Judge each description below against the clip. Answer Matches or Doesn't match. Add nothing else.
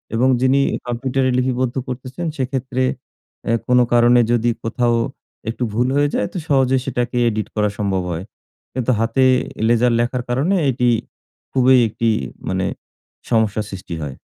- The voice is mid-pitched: Doesn't match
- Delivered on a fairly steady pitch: Matches